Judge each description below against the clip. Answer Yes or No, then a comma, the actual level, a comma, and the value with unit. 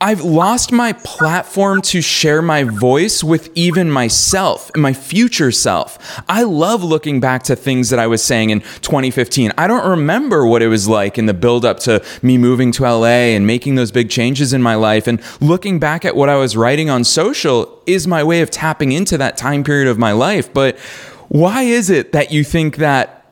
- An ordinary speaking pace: No, fast, 210 wpm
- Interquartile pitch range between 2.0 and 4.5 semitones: No, wide, 5.6 semitones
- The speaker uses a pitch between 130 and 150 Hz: Yes, medium, 140 Hz